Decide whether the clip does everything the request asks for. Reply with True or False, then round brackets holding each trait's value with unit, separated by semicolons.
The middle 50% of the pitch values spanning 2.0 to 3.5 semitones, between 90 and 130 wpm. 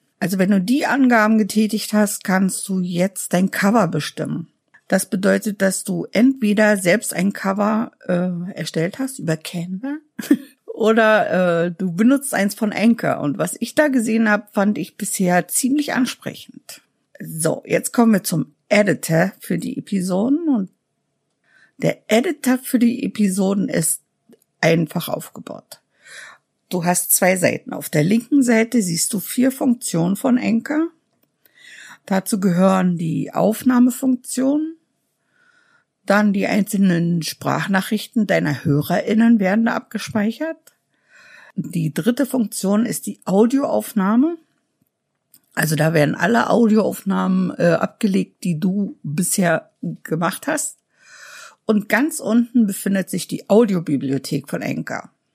False (4.8 semitones; 125 wpm)